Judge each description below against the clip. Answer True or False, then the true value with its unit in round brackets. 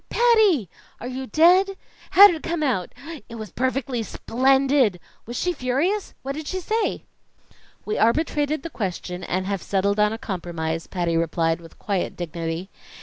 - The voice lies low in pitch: False (245 Hz)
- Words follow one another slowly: False (155 wpm)